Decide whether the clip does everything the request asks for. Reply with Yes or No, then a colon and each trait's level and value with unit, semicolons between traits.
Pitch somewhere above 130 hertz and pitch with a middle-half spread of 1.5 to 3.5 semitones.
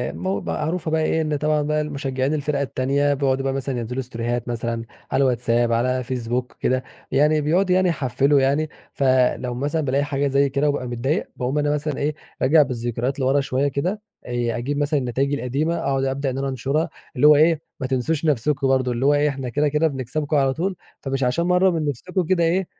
Yes: medium, 140 Hz; average, 2.9 semitones